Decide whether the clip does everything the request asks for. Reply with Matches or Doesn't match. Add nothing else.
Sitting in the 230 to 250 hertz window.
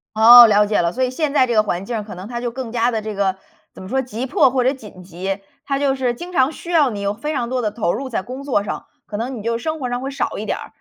Matches